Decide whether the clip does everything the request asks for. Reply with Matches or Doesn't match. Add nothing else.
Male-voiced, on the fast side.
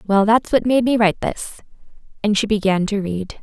Doesn't match